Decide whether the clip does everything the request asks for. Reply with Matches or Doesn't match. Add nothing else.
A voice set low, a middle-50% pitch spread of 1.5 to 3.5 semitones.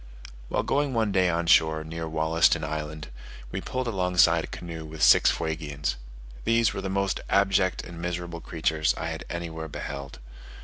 Matches